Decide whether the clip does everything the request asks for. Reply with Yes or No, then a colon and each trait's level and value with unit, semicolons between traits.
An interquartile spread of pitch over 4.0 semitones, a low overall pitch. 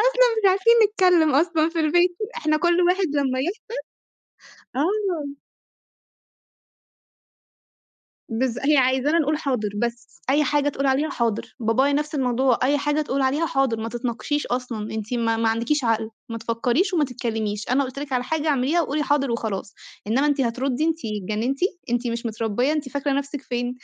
No: average, 4.4 semitones; very high, 270 Hz